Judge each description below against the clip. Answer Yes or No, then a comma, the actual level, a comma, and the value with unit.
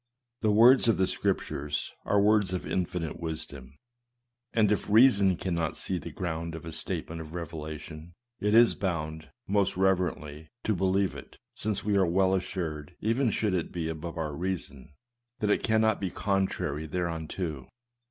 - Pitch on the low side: Yes, very low, 90 Hz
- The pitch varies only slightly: No, average, 4.0 semitones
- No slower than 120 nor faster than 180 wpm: Yes, average, 160 wpm